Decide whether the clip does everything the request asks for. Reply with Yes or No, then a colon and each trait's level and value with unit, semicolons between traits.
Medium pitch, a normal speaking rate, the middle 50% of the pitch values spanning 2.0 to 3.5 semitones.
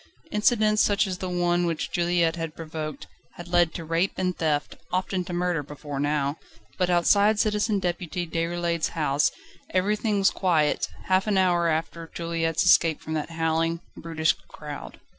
Yes: medium, 170 Hz; average, 160 wpm; narrow, 2.4 semitones